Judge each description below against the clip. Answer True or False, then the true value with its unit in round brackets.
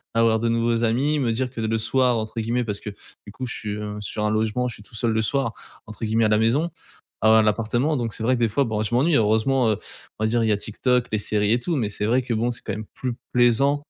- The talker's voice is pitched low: True (115 Hz)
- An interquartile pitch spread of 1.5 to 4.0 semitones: True (2.4 semitones)